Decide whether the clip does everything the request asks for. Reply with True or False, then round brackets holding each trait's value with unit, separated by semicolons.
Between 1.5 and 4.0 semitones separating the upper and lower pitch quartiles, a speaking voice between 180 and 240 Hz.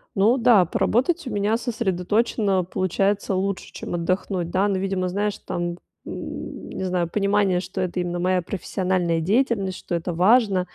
True (2.4 semitones; 190 Hz)